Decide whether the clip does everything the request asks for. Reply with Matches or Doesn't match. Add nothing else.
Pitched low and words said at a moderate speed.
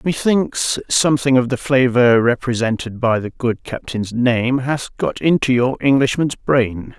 Matches